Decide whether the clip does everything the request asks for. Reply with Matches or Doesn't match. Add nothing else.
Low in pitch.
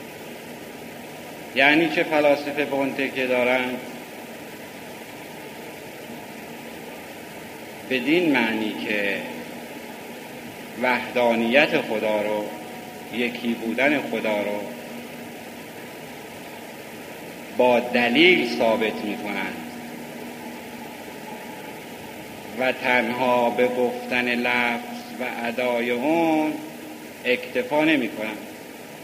Matches